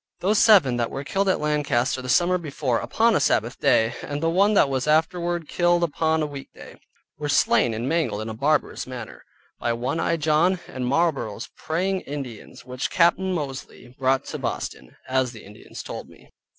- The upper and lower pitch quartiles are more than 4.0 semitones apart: Yes, average, 5.2 semitones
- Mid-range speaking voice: Yes, medium, 145 Hz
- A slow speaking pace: No, average, 185 wpm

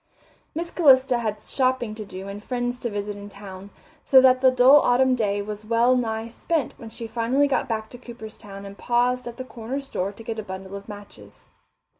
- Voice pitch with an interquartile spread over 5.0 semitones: No, average, 3.7 semitones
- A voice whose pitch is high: Yes, high, 230 Hz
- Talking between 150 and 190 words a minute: No, fast, 205 wpm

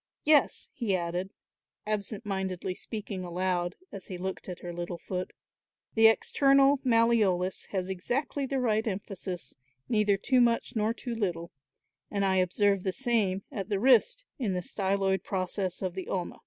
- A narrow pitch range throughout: No, average, 3.7 semitones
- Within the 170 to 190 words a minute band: No, average, 155 wpm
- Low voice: No, high, 195 Hz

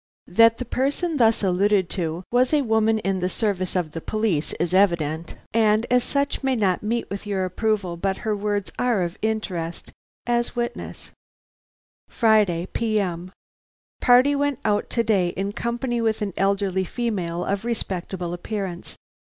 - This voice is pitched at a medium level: No, high, 205 Hz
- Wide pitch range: No, average, 4.0 semitones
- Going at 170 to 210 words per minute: No, average, 155 wpm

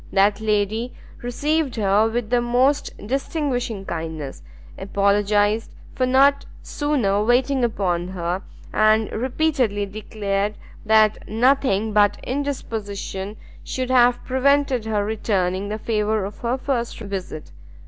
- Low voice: No, high, 220 Hz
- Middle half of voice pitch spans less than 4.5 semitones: Yes, average, 3.9 semitones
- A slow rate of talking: Yes, slow, 115 wpm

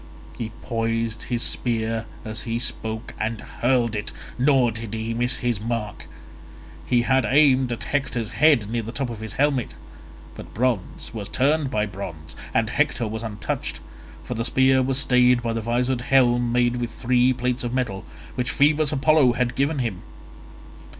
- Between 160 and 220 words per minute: Yes, average, 170 wpm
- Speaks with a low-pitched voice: Yes, low, 120 Hz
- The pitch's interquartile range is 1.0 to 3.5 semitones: Yes, narrow, 2.4 semitones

